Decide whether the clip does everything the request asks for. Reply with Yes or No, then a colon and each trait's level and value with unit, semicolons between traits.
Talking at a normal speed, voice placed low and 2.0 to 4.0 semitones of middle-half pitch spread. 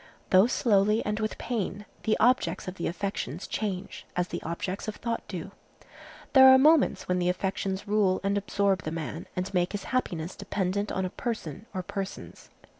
No: average, 180 wpm; high, 195 Hz; average, 2.8 semitones